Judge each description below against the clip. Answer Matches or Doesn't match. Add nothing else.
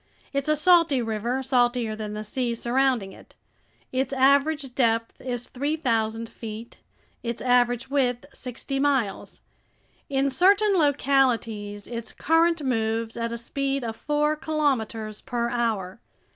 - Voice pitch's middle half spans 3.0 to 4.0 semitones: Matches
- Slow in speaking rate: Matches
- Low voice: Doesn't match